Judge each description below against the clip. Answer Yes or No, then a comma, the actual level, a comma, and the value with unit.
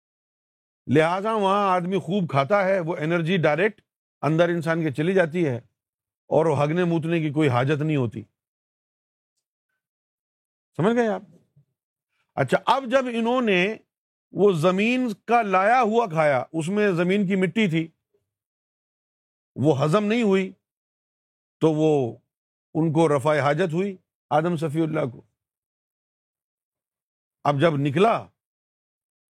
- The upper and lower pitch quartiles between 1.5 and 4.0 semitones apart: No, average, 4.8 semitones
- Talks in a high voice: No, medium, 175 Hz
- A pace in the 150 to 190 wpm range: No, average, 125 wpm